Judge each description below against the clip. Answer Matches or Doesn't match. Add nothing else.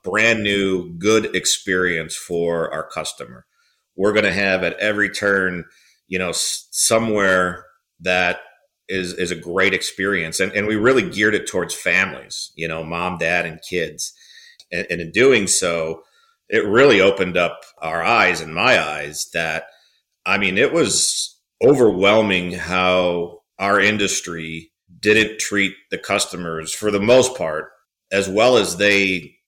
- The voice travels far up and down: Doesn't match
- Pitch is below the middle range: Matches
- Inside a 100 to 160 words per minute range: Matches